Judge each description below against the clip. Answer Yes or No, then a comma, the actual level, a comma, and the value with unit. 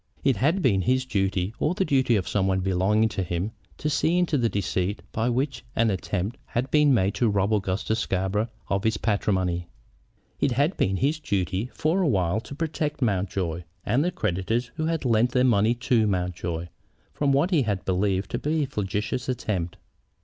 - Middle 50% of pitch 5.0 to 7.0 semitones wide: Yes, wide, 5.6 semitones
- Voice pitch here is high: No, low, 110 Hz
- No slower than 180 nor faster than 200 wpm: Yes, average, 190 wpm